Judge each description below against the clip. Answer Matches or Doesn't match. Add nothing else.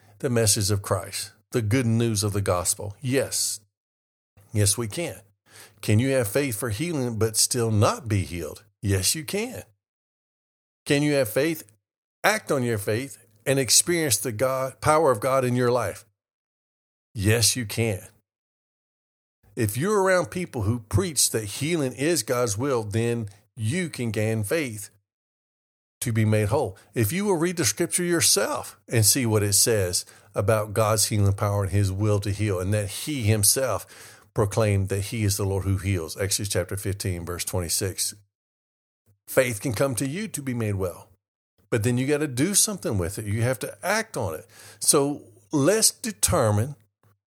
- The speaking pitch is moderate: Doesn't match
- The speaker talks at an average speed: Matches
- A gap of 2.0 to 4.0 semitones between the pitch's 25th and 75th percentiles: Doesn't match